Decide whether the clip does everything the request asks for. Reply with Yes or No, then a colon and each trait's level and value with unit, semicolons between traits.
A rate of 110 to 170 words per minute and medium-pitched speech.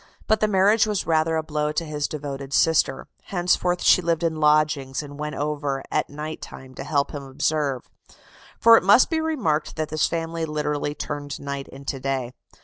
No: average, 185 wpm; medium, 150 Hz